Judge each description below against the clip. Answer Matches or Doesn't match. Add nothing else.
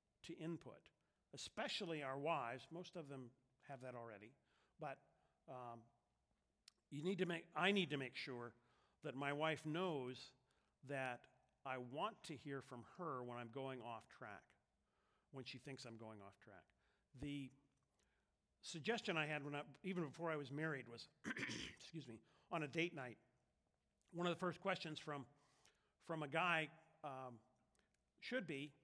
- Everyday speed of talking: Matches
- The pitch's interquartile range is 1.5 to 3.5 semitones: Doesn't match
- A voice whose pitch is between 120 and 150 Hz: Matches